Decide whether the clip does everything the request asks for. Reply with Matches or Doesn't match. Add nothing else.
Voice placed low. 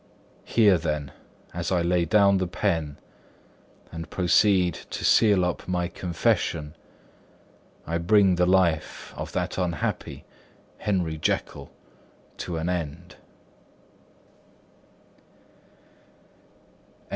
Matches